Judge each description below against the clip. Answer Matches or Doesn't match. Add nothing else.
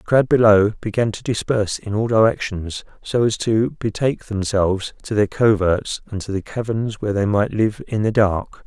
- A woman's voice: Doesn't match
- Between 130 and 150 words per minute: Doesn't match